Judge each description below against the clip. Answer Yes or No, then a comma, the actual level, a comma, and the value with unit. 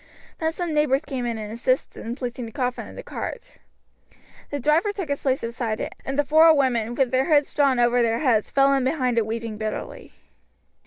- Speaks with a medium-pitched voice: No, very high, 255 Hz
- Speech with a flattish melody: No, average, 3.7 semitones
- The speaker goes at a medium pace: No, fast, 210 wpm